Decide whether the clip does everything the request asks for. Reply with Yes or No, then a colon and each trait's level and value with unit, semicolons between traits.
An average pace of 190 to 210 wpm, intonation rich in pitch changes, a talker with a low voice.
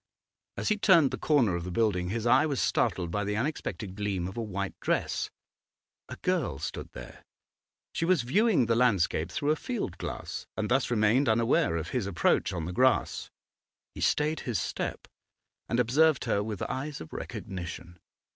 No: average, 175 wpm; wide, 6.7 semitones; low, 115 Hz